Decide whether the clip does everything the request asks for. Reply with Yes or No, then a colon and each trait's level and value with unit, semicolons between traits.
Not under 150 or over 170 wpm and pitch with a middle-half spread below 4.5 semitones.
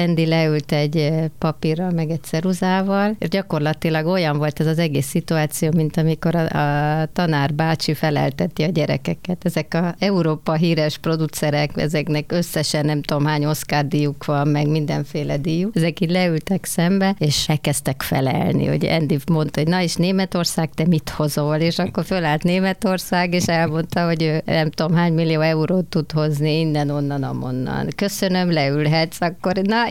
Yes: average, 160 wpm; narrow, 2.4 semitones